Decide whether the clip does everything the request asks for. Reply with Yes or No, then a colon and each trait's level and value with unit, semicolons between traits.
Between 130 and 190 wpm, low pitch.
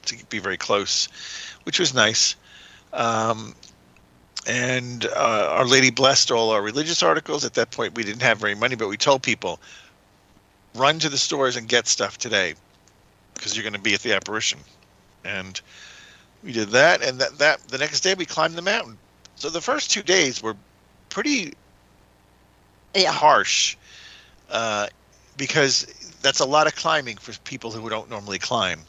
Yes: average, 170 wpm; low, 120 Hz